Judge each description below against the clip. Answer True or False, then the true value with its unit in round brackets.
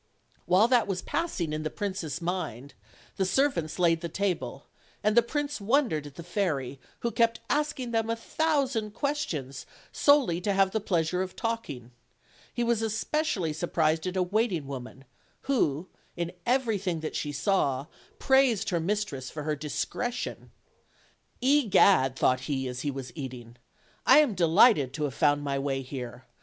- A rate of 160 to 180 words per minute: True (165 wpm)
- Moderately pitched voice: True (180 Hz)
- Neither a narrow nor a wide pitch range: False (8.1 semitones)